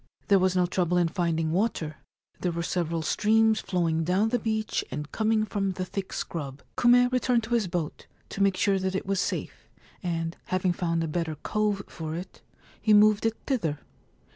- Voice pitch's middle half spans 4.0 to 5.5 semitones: Yes, average, 4.3 semitones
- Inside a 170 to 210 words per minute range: Yes, average, 190 wpm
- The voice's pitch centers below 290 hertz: Yes, medium, 185 Hz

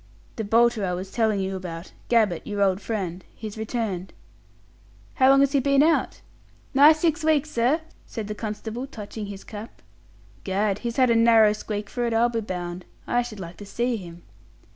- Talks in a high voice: Yes, high, 220 Hz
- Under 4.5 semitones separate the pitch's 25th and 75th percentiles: Yes, average, 3.6 semitones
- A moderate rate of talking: Yes, average, 185 wpm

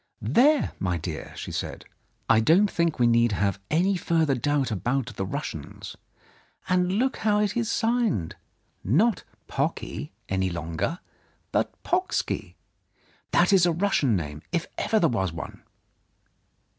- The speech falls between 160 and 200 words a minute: No, average, 145 wpm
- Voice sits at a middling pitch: Yes, medium, 150 Hz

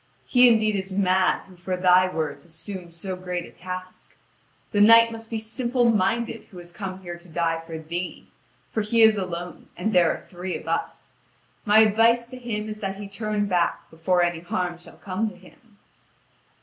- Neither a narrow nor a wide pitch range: Yes, average, 3.6 semitones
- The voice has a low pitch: No, high, 190 Hz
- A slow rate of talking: No, average, 190 wpm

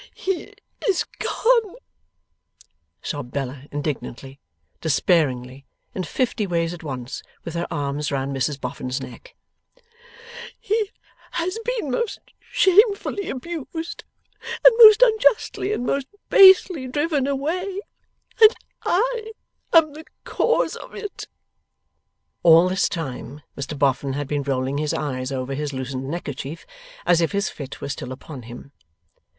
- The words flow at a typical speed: No, slow, 125 wpm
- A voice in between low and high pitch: Yes, medium, 165 Hz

